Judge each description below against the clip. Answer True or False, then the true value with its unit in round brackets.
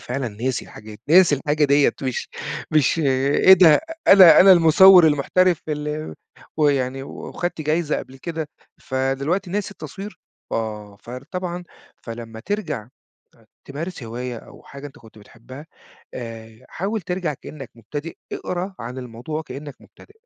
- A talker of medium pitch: True (145 Hz)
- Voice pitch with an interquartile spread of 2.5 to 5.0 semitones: False (5.4 semitones)